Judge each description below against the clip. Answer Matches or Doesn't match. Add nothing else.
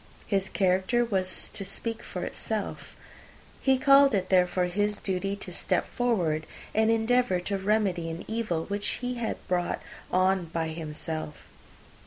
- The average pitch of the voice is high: Matches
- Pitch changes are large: Doesn't match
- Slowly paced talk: Doesn't match